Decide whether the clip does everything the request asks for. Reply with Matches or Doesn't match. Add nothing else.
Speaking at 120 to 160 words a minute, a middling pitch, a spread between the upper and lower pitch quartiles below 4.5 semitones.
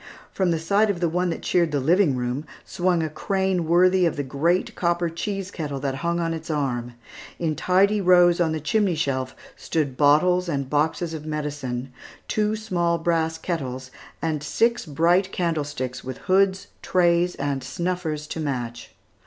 Doesn't match